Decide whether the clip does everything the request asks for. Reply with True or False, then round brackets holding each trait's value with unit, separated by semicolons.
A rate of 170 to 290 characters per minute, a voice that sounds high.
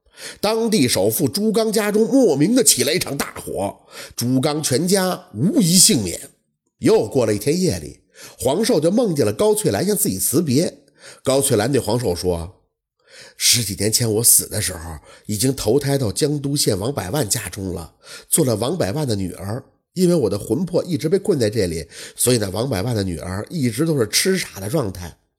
False (270 characters per minute; 130 Hz)